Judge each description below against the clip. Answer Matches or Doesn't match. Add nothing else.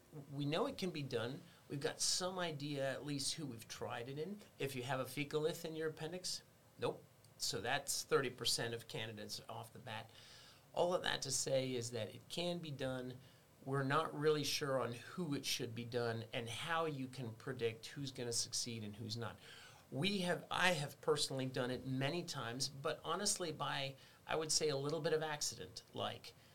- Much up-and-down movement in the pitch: Doesn't match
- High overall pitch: Doesn't match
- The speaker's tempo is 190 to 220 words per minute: Matches